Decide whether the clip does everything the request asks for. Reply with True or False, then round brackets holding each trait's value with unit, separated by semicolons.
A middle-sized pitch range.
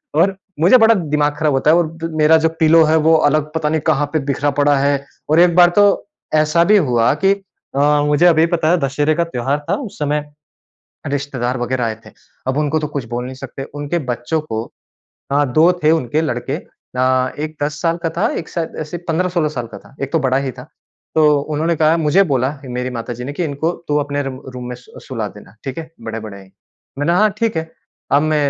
True (3.5 semitones)